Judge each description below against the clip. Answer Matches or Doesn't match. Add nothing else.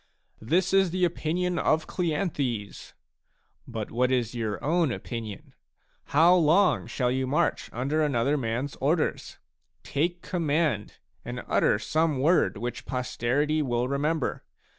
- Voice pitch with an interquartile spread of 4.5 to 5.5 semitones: Matches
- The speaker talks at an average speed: Doesn't match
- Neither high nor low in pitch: Matches